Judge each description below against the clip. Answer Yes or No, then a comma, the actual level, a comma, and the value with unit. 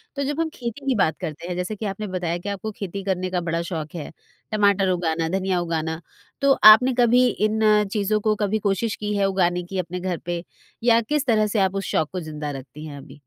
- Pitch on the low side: No, high, 190 Hz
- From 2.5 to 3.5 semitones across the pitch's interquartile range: No, average, 3.9 semitones